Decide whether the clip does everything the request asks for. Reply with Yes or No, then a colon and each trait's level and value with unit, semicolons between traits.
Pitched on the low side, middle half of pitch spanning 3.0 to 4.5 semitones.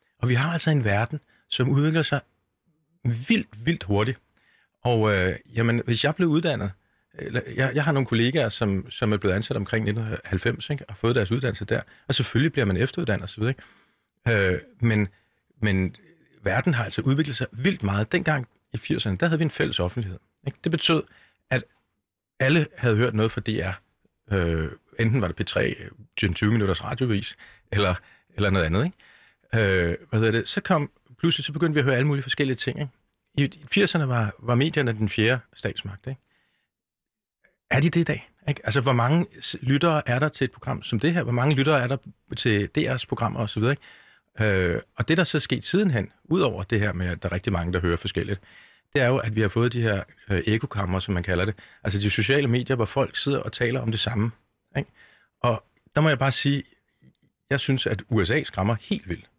No: low, 120 Hz; average, 5.2 semitones